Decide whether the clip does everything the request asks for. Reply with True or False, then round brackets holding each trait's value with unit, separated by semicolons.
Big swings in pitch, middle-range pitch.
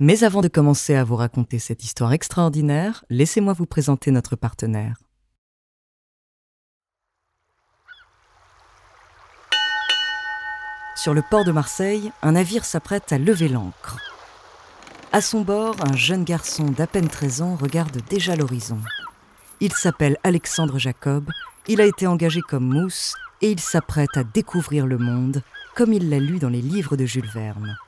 True (5.7 semitones; 160 Hz)